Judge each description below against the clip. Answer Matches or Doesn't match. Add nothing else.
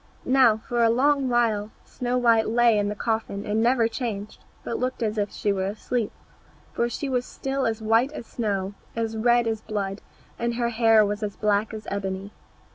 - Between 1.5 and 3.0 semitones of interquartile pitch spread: Matches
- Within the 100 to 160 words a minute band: Doesn't match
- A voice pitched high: Matches